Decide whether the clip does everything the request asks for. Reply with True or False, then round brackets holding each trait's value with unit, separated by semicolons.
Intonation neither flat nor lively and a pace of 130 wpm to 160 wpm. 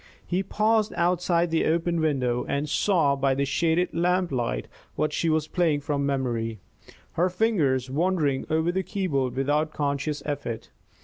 True (4.2 semitones; 145 wpm)